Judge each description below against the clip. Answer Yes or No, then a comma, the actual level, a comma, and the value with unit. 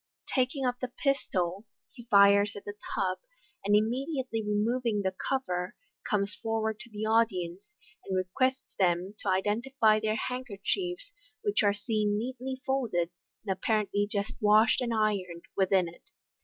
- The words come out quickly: No, average, 150 wpm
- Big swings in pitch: No, average, 3.9 semitones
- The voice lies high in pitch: Yes, high, 215 Hz